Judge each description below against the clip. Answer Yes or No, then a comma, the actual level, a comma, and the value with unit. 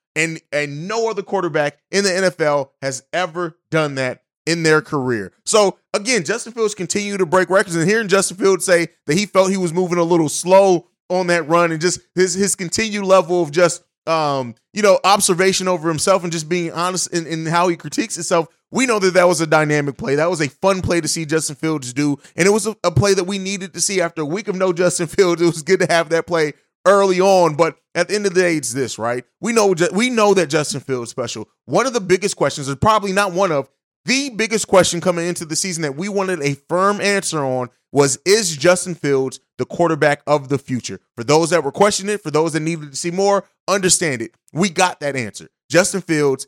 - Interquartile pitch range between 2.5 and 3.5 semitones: No, average, 4.0 semitones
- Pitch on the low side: No, medium, 175 Hz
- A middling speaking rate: No, fast, 235 wpm